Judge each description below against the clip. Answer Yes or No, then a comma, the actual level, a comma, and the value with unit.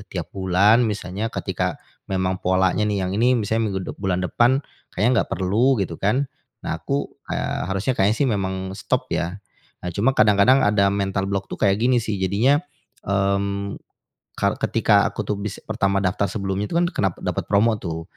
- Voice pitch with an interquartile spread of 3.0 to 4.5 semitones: No, narrow, 2.6 semitones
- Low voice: Yes, low, 100 Hz